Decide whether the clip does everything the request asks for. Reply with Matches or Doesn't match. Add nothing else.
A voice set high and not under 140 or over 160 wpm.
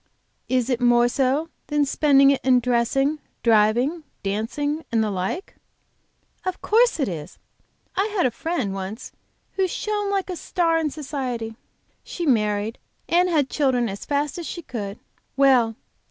Matches